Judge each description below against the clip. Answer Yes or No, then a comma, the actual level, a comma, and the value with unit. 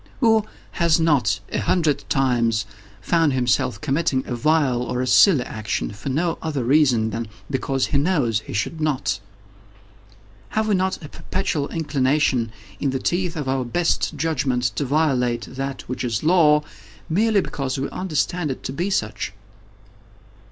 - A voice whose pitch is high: No, medium, 140 Hz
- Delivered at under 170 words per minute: Yes, average, 155 wpm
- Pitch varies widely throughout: No, average, 4.6 semitones